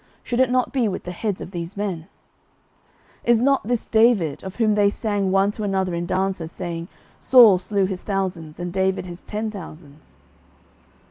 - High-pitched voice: Yes, high, 195 Hz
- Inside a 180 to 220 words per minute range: Yes, average, 185 wpm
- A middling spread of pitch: Yes, average, 3.5 semitones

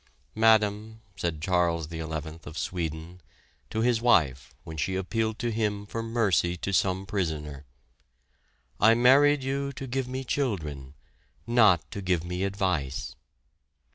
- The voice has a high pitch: No, very low, 95 Hz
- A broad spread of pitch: Yes, wide, 5.8 semitones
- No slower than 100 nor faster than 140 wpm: Yes, slow, 135 wpm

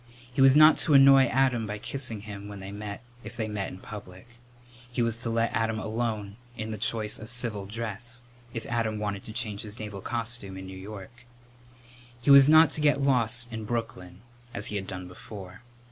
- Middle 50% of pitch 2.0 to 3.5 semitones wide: Yes, average, 2.8 semitones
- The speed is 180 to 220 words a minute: Yes, average, 200 wpm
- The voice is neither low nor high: No, low, 110 Hz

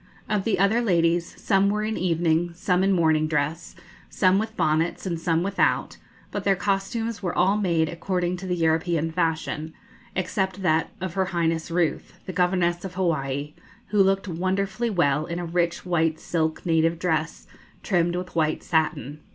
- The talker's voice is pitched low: No, medium, 175 Hz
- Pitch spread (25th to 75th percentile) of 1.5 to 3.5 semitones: Yes, average, 2.8 semitones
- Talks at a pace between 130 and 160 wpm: No, average, 170 wpm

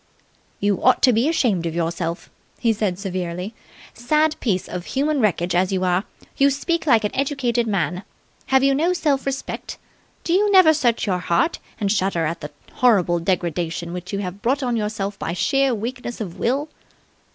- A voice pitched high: Yes, high, 215 Hz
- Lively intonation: Yes, wide, 7.1 semitones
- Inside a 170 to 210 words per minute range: Yes, average, 180 wpm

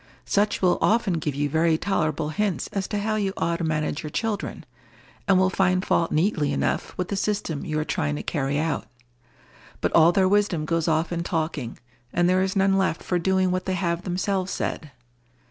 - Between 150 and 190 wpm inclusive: No, average, 200 wpm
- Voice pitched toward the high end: No, medium, 175 Hz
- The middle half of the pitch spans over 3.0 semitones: Yes, average, 3.5 semitones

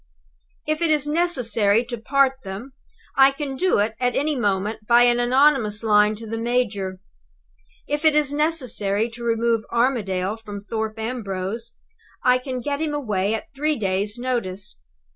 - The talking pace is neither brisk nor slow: Yes, average, 160 wpm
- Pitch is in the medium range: No, high, 235 Hz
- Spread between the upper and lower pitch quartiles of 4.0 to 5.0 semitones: Yes, average, 4.5 semitones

